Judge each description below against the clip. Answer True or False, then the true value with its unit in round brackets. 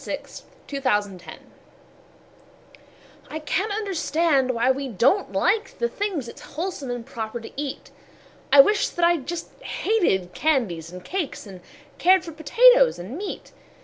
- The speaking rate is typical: True (150 wpm)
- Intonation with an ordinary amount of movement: False (8.1 semitones)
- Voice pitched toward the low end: False (290 Hz)